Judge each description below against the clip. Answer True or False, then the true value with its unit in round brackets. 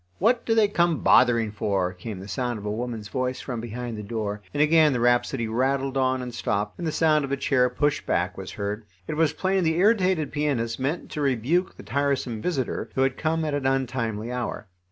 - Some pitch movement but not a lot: True (4.8 semitones)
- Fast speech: True (215 wpm)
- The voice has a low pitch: True (130 Hz)